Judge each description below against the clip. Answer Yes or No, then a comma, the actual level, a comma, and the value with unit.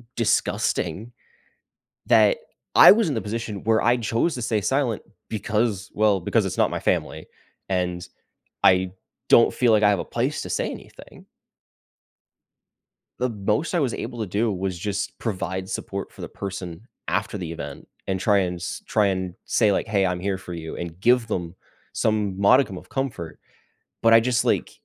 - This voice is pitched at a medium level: No, low, 105 Hz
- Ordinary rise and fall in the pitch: Yes, average, 3.7 semitones